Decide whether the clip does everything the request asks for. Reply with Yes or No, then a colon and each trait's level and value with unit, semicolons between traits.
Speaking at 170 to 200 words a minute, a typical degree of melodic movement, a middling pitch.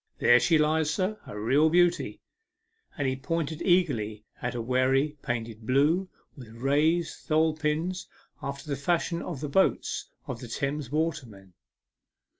No: average, 145 wpm; average, 4.6 semitones; medium, 145 Hz